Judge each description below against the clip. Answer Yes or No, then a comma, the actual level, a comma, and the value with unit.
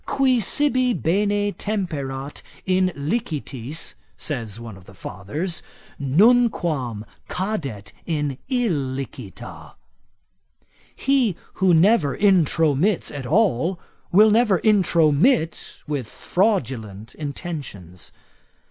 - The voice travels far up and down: Yes, wide, 7.5 semitones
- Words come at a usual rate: No, slow, 85 wpm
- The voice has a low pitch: No, medium, 160 Hz